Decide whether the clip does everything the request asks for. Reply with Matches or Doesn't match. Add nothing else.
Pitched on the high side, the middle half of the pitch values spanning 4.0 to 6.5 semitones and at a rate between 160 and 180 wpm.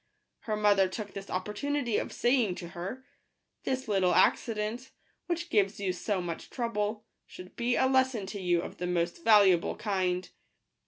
Matches